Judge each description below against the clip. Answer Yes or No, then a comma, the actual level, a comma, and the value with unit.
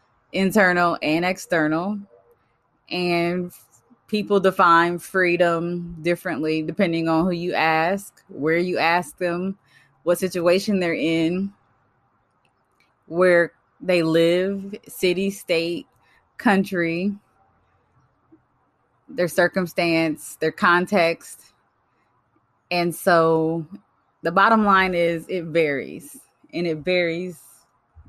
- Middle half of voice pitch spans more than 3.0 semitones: No, narrow, 2.4 semitones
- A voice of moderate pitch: Yes, medium, 175 Hz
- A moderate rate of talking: No, slow, 90 wpm